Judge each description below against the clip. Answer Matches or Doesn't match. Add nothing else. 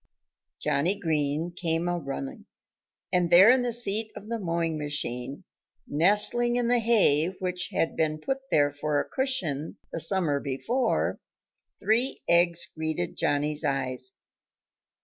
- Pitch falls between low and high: Matches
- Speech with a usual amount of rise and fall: Doesn't match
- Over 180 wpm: Doesn't match